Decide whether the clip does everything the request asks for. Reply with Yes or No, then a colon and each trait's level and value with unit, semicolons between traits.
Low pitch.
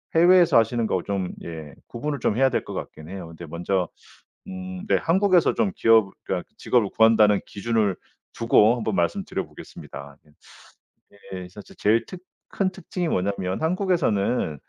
Yes: low, 110 Hz